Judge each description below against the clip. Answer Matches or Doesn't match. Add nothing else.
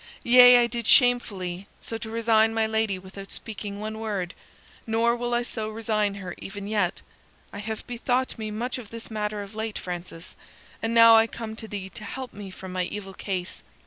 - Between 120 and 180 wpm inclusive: Doesn't match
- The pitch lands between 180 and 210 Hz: Doesn't match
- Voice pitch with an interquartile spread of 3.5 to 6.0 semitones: Doesn't match